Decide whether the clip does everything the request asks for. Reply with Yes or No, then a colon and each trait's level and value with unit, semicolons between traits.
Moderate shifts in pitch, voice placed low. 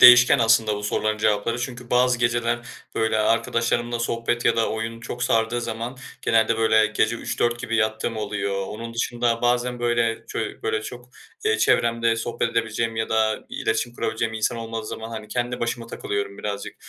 No: narrow, 1.3 semitones; low, 115 Hz